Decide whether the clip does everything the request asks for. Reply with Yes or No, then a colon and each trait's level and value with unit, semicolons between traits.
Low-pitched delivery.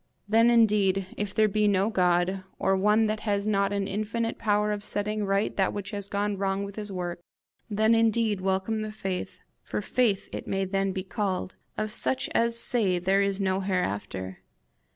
No: high, 200 Hz